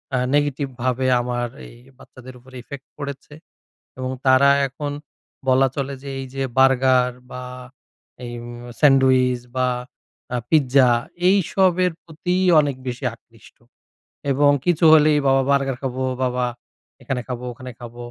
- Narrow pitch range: Yes, narrow, 2.1 semitones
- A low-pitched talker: Yes, low, 130 Hz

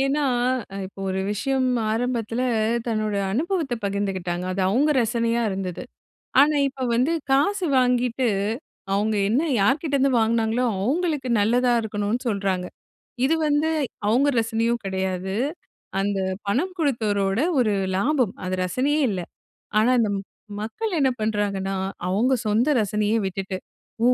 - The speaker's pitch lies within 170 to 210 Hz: No, high, 230 Hz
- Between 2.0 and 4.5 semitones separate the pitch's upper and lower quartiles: No, average, 5.0 semitones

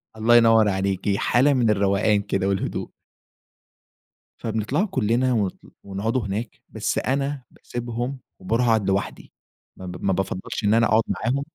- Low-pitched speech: Yes, low, 110 Hz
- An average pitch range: Yes, average, 3.5 semitones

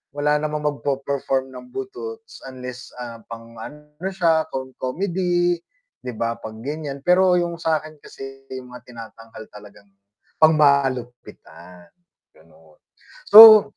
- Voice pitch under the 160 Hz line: Yes, medium, 140 Hz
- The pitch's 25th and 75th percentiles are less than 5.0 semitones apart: No, average, 5.3 semitones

